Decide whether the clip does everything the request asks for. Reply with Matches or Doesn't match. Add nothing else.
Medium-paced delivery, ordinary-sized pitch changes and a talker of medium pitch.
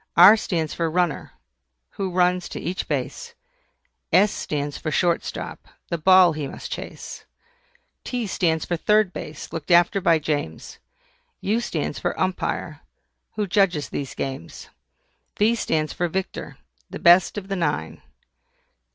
Matches